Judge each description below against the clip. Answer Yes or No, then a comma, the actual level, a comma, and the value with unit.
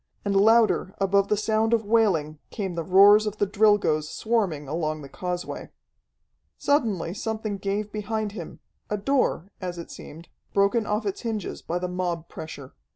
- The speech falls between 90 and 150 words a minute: No, average, 160 wpm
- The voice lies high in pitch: Yes, high, 200 Hz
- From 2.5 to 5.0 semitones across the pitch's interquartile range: Yes, average, 3.6 semitones